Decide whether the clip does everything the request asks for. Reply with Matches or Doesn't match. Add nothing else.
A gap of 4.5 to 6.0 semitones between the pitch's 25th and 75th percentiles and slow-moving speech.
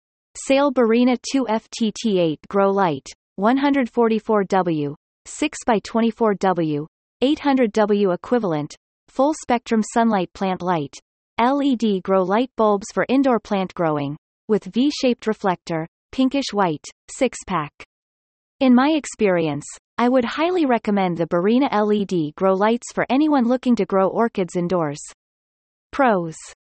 Matches